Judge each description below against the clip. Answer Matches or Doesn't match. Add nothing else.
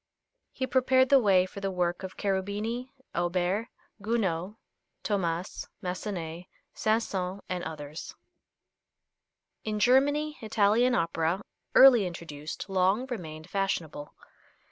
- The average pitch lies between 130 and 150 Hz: Doesn't match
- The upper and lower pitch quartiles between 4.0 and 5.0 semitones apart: Matches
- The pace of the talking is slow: Matches